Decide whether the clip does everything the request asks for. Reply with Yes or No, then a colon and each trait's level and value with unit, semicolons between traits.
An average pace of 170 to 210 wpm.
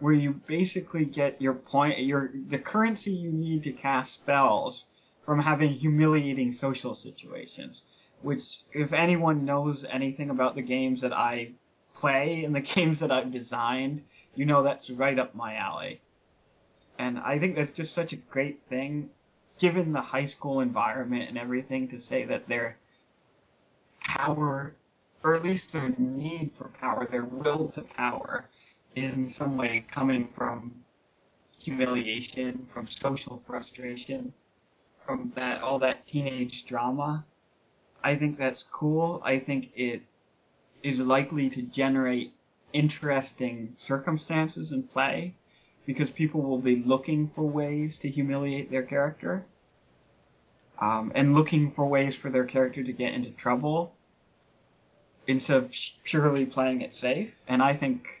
No: average, 140 wpm